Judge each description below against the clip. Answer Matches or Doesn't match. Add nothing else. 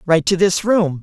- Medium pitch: Matches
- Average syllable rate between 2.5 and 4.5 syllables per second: Matches